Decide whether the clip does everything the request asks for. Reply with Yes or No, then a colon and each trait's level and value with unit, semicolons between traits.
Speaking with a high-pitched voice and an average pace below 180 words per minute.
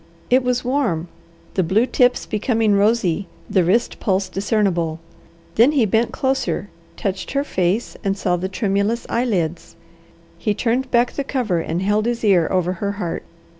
Yes: high, 205 Hz; average, 160 wpm